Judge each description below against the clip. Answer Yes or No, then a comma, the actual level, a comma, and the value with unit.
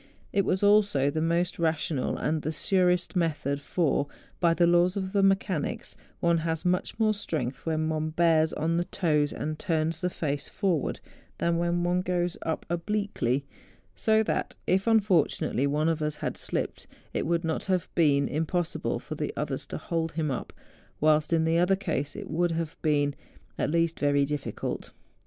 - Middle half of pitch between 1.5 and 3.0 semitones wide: Yes, average, 2.7 semitones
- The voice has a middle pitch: Yes, medium, 165 Hz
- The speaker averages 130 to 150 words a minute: No, average, 175 wpm